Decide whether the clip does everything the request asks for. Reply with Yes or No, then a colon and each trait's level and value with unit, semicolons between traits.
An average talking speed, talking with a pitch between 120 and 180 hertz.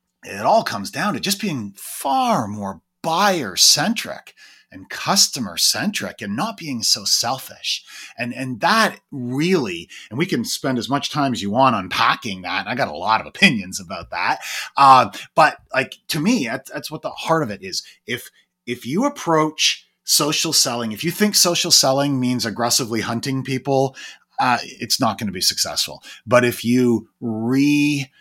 Yes: average, 175 wpm; low, 135 Hz